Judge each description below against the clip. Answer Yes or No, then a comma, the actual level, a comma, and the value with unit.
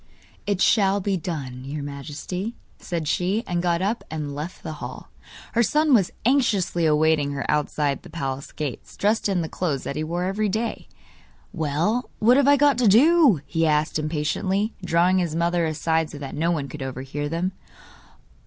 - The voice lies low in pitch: No, medium, 170 Hz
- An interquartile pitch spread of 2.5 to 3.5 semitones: No, average, 5.1 semitones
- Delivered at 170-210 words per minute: Yes, average, 180 wpm